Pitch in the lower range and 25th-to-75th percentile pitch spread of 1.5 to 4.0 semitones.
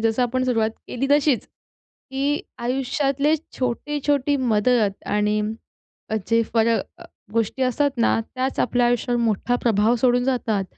No: high, 245 Hz; average, 2.9 semitones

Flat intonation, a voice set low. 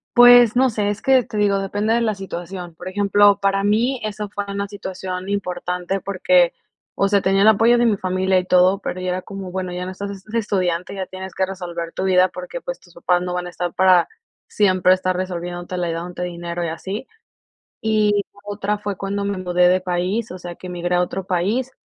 No: narrow, 2.3 semitones; high, 190 Hz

